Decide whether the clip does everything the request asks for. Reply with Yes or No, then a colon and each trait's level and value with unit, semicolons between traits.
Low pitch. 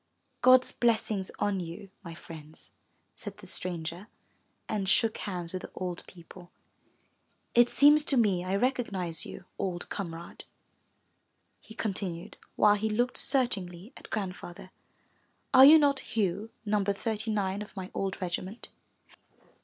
No: high, 195 Hz